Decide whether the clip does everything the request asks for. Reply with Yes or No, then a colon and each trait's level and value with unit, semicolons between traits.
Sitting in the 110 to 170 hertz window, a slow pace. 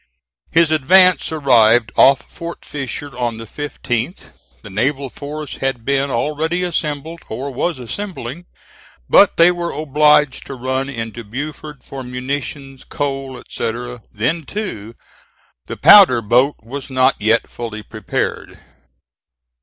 Yes: low, 135 Hz; slow, 125 wpm